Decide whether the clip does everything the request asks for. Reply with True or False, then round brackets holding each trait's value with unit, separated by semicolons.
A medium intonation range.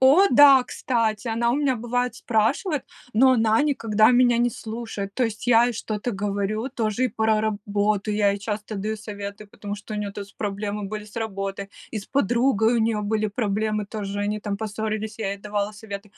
False (2.3 semitones)